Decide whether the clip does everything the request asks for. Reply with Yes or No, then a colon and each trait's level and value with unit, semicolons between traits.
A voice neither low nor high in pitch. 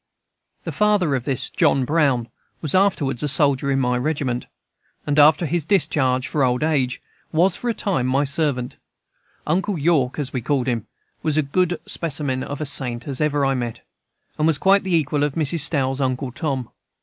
Yes: medium, 145 Hz